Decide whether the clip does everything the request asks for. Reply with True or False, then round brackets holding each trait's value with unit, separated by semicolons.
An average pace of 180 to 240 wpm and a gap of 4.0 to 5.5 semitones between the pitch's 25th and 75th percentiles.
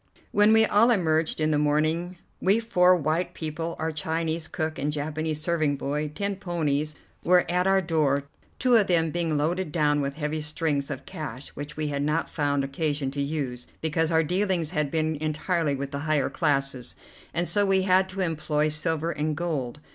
False (185 wpm; 2.8 semitones)